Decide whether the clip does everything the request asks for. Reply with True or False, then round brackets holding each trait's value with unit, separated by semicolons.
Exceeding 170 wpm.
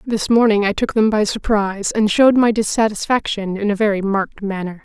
True (200 wpm)